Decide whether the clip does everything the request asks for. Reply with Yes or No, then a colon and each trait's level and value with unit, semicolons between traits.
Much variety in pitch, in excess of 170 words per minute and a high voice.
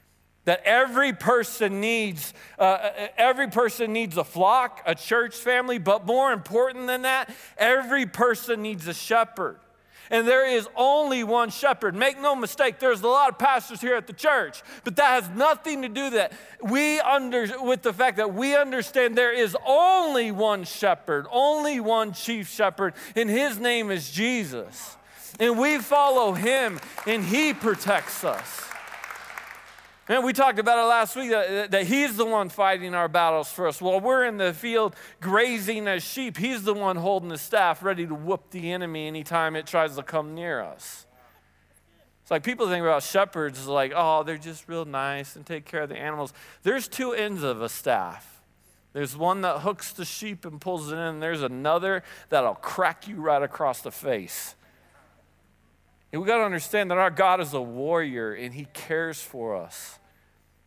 Yes: wide, 6.9 semitones; average, 180 wpm; high, 210 Hz